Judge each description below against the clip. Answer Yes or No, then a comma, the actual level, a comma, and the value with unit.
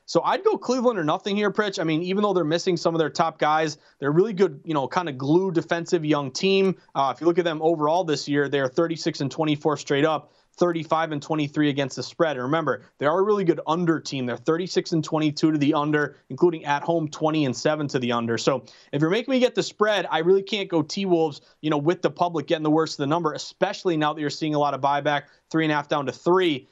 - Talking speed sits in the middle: No, fast, 265 wpm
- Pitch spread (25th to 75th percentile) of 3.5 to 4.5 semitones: No, average, 3.1 semitones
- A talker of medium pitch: Yes, medium, 160 Hz